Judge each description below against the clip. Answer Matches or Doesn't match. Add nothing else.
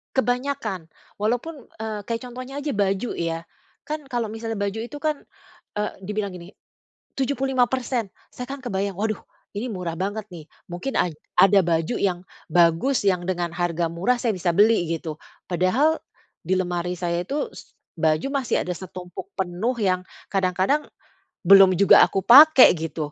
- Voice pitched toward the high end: Matches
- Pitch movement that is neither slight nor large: Doesn't match